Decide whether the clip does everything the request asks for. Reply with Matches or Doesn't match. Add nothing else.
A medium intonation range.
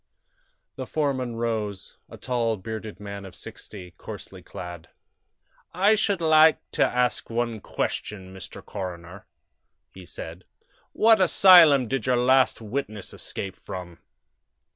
Doesn't match